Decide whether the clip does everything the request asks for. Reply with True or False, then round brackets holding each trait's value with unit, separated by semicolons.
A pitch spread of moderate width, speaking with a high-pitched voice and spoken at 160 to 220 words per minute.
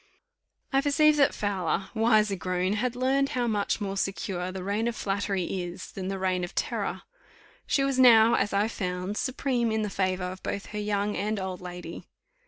True (3.8 semitones; 205 Hz; 190 wpm)